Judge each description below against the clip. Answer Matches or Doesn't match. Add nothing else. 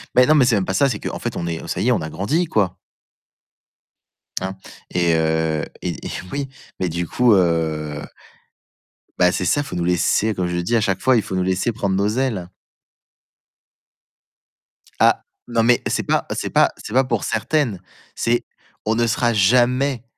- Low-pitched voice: Matches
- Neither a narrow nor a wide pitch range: Doesn't match